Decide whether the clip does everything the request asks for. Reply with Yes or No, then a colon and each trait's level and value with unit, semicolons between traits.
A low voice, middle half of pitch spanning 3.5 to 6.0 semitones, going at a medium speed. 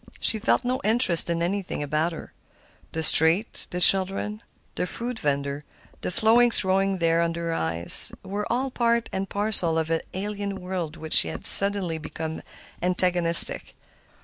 No: medium, 180 Hz; average, 4.0 semitones; average, 150 wpm